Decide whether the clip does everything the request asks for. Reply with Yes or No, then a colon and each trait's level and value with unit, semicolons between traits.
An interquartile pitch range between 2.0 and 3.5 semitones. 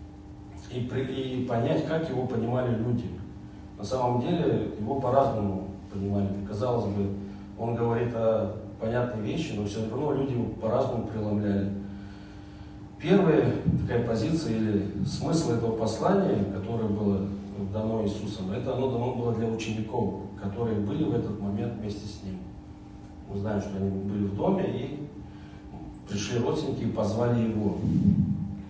Yes: average, 2.9 semitones